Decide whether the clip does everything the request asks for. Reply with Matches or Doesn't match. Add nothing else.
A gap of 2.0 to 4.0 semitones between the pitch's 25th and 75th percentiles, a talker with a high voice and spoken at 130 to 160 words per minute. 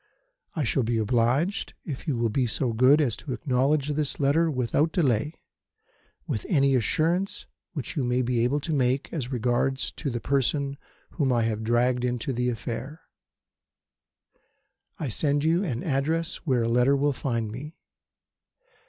Doesn't match